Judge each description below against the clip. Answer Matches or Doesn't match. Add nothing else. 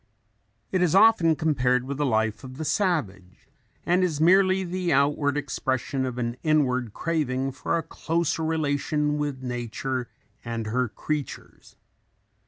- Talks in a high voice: Doesn't match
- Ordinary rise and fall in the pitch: Matches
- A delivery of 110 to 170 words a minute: Matches